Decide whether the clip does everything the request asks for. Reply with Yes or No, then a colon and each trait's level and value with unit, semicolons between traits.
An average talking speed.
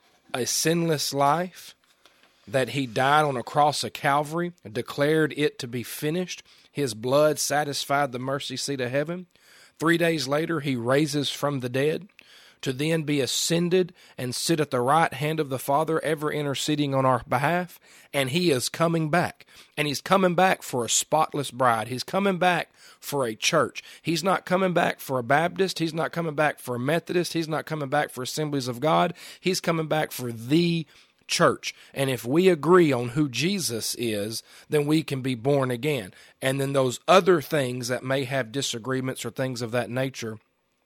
Yes: average, 185 wpm